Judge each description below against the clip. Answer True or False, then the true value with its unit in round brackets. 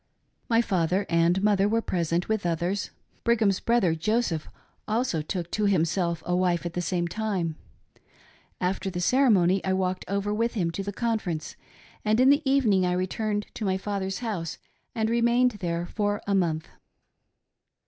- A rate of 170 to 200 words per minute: False (160 wpm)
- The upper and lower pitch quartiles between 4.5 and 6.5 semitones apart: False (3.9 semitones)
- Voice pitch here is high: True (195 Hz)